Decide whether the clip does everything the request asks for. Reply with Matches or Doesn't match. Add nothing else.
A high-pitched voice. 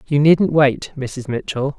Doesn't match